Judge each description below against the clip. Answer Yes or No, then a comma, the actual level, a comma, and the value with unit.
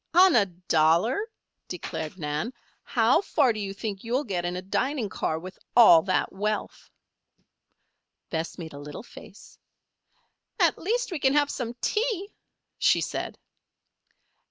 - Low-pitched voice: No, high, 215 Hz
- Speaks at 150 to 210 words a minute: No, average, 140 wpm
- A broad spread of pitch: Yes, wide, 8.1 semitones